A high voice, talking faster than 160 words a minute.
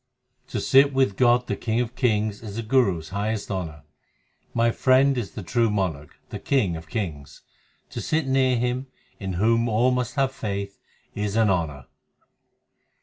No: low, 110 Hz; average, 170 wpm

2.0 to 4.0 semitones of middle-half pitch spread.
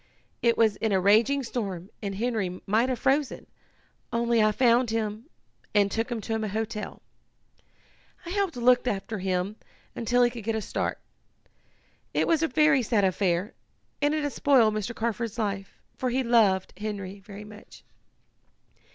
Yes: average, 3.2 semitones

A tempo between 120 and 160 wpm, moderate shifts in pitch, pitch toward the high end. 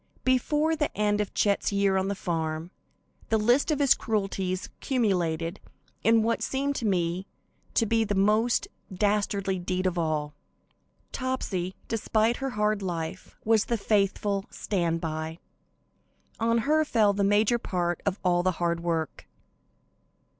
Yes: average, 145 wpm; average, 4.2 semitones; high, 200 Hz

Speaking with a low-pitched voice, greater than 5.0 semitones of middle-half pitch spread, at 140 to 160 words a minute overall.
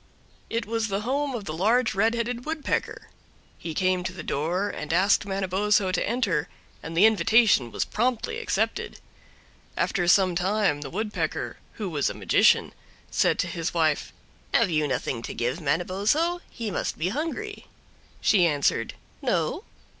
No: high, 195 Hz; wide, 5.4 semitones; average, 155 wpm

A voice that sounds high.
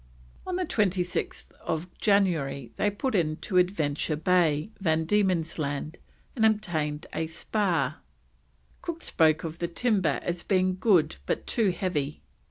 No: medium, 175 Hz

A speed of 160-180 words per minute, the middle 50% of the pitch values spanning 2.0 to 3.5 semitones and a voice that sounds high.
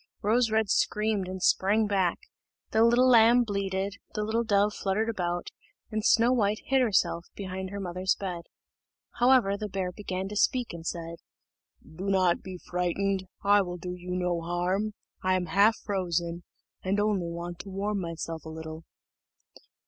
Yes: average, 165 wpm; average, 3.0 semitones; high, 195 Hz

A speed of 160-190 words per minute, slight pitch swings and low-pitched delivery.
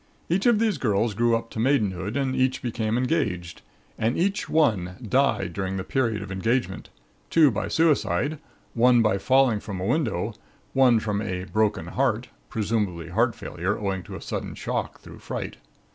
No: average, 165 wpm; average, 5.1 semitones; low, 115 Hz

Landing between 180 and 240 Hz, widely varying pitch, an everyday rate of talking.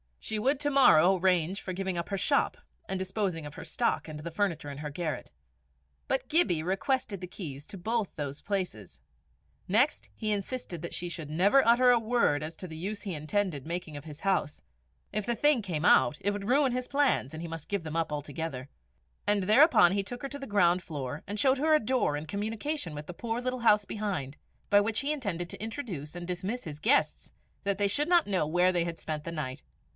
No: high, 190 Hz; wide, 5.9 semitones; fast, 220 wpm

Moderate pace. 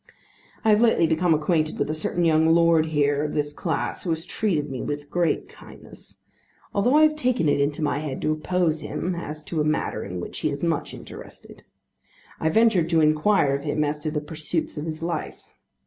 No: fast, 210 wpm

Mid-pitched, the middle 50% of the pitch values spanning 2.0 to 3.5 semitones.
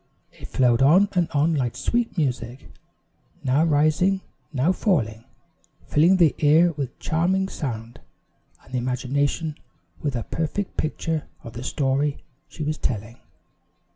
No: medium, 145 Hz; average, 4.6 semitones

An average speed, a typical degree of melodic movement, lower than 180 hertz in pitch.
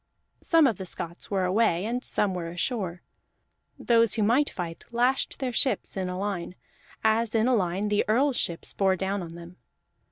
No: average, 185 wpm; average, 4.4 semitones; high, 205 Hz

